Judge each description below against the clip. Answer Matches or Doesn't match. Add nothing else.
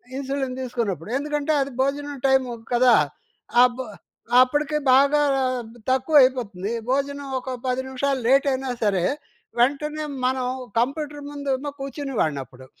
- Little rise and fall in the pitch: Matches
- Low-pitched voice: Doesn't match